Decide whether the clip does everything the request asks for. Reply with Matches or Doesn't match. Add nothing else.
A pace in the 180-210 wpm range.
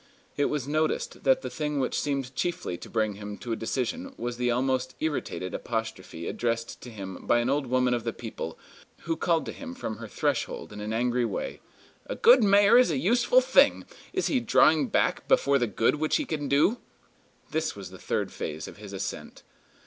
Matches